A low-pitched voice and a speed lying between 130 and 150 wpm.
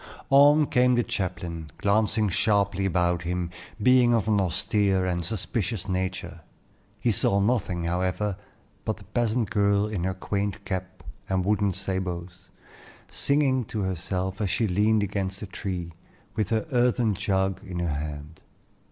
Yes: low, 100 Hz; average, 145 wpm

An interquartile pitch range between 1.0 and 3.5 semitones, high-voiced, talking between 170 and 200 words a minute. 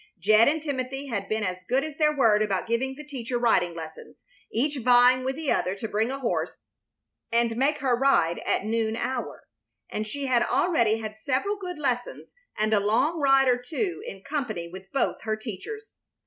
No: average, 4.3 semitones; high, 245 Hz; average, 190 wpm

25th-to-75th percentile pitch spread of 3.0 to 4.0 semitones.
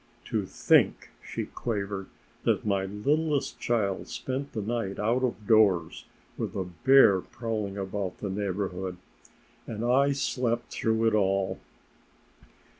Yes: average, 3.6 semitones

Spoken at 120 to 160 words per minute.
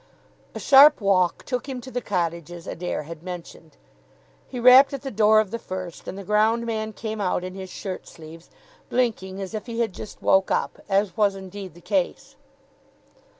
No: average, 190 wpm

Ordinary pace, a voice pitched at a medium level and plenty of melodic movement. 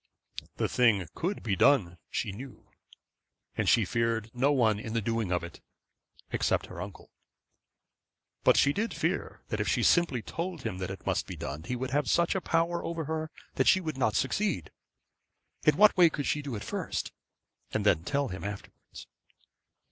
No: average, 185 wpm; low, 125 Hz; wide, 7.5 semitones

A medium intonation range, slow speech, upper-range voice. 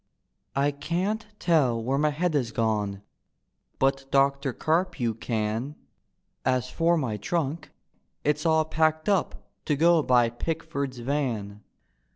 No: average, 4.9 semitones; slow, 130 wpm; medium, 140 Hz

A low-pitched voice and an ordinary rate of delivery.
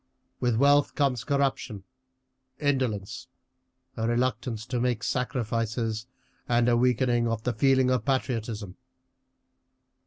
No: low, 120 Hz; slow, 105 wpm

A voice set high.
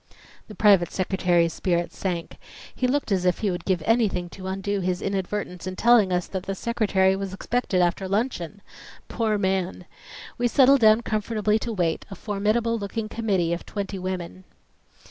Yes: high, 195 Hz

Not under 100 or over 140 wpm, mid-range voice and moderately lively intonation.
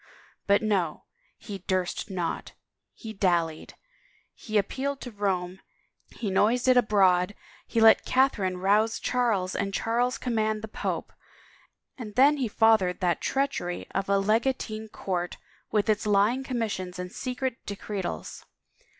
No: slow, 135 wpm; high, 210 Hz; average, 3.8 semitones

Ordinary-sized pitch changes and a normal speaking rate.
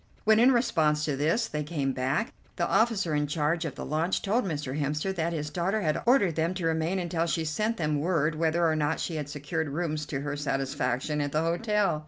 No: average, 3.0 semitones; fast, 220 wpm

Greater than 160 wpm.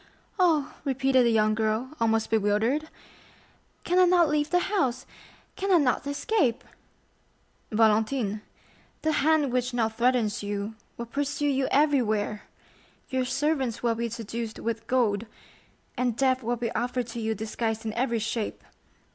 No: average, 140 wpm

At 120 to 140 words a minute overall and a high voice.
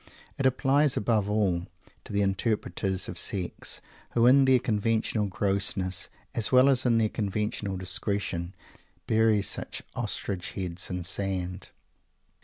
No: slow, 135 wpm; low, 100 Hz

